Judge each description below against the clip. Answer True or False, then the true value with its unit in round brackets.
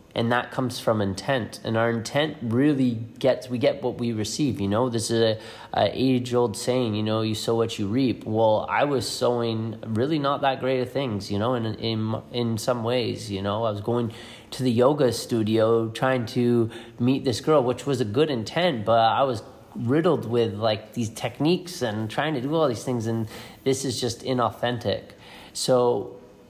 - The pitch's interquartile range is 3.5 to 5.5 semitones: False (2.4 semitones)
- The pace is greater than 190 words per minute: True (200 wpm)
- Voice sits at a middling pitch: False (120 Hz)